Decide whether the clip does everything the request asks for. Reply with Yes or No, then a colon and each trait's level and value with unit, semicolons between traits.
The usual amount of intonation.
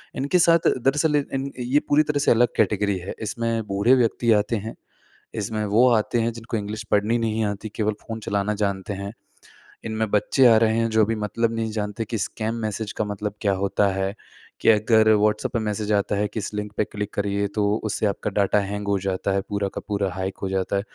No: narrow, 1.9 semitones